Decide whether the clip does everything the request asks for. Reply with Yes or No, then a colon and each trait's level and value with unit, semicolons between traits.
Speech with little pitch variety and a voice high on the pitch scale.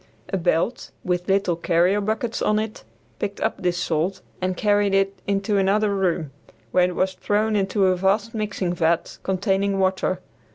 Yes: narrow, 2.2 semitones; high, 195 Hz